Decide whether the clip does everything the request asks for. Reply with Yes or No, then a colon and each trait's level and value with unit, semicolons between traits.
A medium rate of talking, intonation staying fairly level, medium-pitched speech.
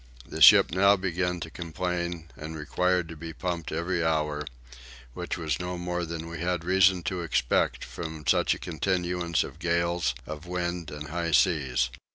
No: average, 170 wpm; narrow, 2.0 semitones; very low, 85 Hz